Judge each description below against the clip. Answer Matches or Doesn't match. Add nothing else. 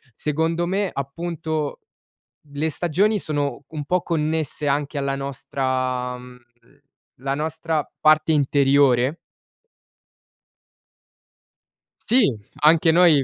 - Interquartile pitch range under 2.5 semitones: Doesn't match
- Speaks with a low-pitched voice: Doesn't match